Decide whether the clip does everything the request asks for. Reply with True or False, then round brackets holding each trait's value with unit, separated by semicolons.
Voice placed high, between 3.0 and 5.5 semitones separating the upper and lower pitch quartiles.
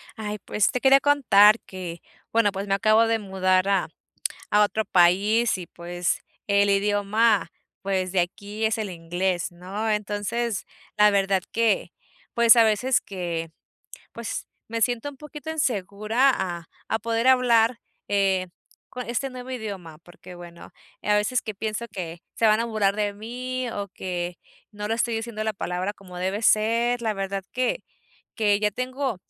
True (210 Hz; 3.3 semitones)